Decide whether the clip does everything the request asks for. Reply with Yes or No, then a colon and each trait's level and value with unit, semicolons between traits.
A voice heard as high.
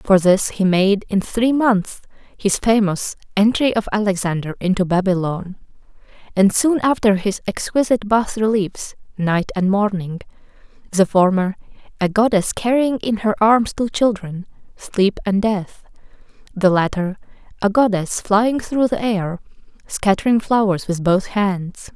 Yes: high, 205 Hz